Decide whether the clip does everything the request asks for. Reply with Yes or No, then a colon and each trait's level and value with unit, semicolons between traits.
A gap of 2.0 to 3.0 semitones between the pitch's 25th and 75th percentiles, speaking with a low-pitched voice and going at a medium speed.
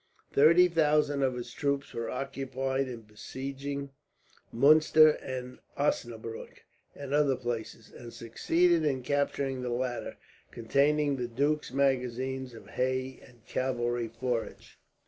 No: average, 2.7 semitones; low, 130 Hz; slow, 120 wpm